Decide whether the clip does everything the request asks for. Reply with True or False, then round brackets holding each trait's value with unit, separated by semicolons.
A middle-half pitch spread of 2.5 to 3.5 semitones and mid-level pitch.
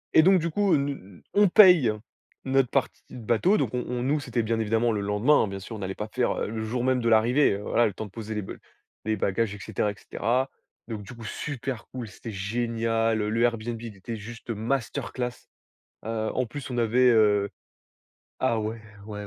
False (2.9 semitones; 115 Hz)